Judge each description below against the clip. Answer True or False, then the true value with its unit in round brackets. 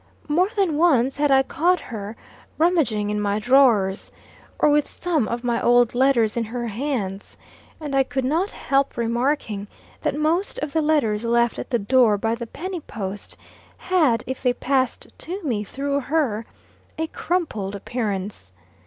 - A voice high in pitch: True (255 Hz)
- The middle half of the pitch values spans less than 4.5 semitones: False (5.4 semitones)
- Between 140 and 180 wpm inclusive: True (160 wpm)